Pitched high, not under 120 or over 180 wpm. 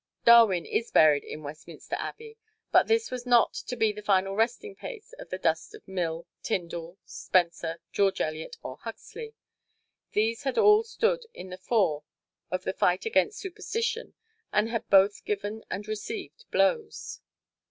Yes: high, 220 Hz; average, 155 wpm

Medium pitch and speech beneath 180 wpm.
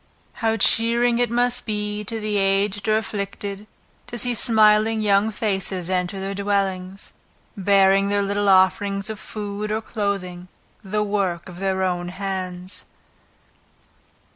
No: high, 200 Hz; slow, 135 wpm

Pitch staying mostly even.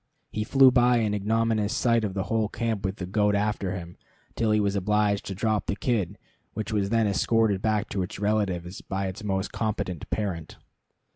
Yes: narrow, 2.3 semitones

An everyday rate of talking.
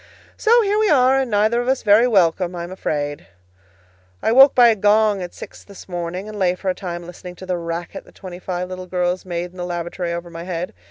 No: fast, 235 wpm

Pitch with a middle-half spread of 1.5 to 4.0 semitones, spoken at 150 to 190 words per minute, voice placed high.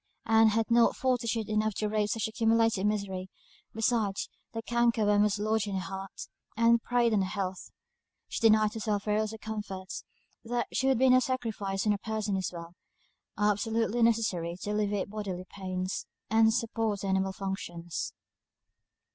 Yes: narrow, 2.5 semitones; average, 165 wpm; high, 215 Hz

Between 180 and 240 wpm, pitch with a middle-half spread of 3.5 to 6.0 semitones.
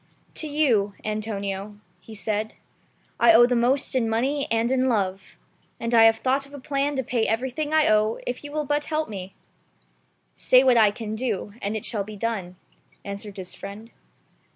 Yes: average, 185 wpm; average, 4.1 semitones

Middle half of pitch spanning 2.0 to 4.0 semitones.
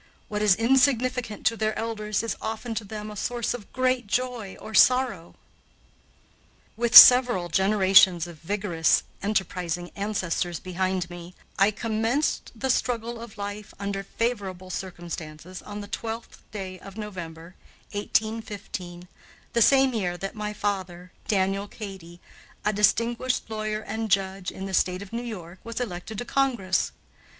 Yes: average, 3.6 semitones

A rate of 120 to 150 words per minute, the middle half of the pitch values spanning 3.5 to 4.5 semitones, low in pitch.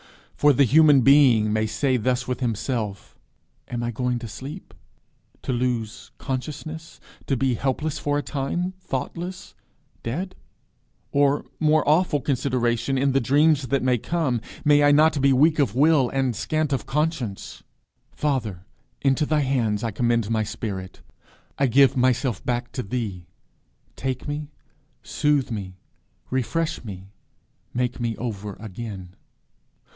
Yes: average, 140 wpm; average, 4.0 semitones; low, 130 Hz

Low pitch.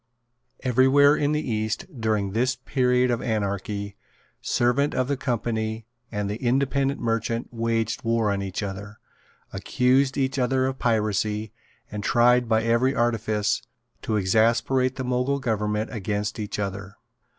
Yes: low, 115 Hz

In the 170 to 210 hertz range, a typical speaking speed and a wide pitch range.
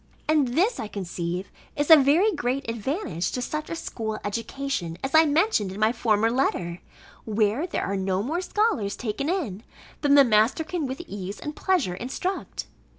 No: very high, 250 Hz; average, 175 wpm; wide, 7.1 semitones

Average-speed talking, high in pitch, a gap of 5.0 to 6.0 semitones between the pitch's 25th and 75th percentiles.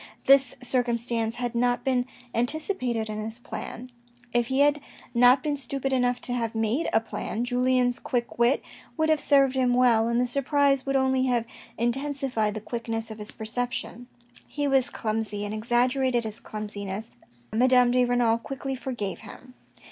No: average, 165 wpm; high, 245 Hz; narrow, 2.5 semitones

